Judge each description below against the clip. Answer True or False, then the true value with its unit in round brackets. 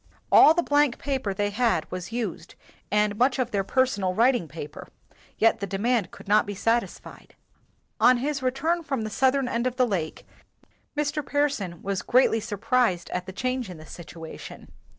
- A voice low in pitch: False (230 Hz)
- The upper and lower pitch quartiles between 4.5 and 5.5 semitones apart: True (5.0 semitones)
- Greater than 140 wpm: True (175 wpm)